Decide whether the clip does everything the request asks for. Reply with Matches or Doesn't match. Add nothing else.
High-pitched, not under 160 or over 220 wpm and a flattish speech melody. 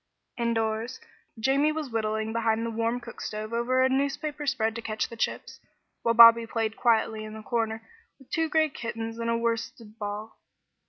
Matches